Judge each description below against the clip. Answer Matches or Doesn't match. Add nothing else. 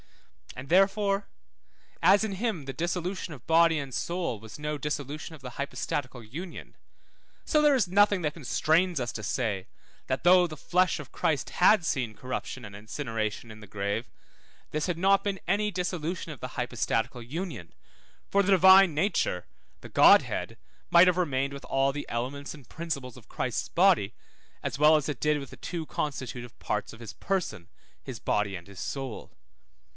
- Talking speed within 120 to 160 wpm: Doesn't match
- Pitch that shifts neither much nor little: Doesn't match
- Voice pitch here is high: Doesn't match